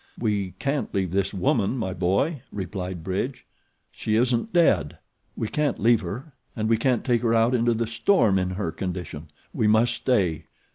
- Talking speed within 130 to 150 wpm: No, average, 175 wpm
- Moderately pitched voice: No, low, 110 Hz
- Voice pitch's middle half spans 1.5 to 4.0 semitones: No, average, 4.5 semitones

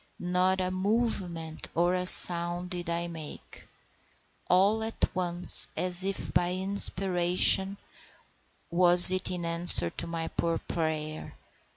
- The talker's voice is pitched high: No, medium, 180 Hz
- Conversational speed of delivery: No, slow, 115 wpm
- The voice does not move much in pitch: Yes, narrow, 1.6 semitones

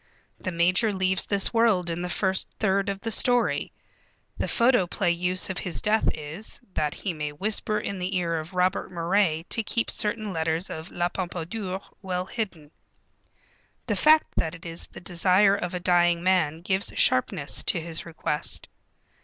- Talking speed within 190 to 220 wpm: No, average, 170 wpm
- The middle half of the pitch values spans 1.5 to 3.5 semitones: Yes, average, 2.9 semitones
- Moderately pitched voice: Yes, medium, 180 Hz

